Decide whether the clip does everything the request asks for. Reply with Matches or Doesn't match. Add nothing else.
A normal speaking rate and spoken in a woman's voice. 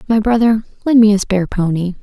Doesn't match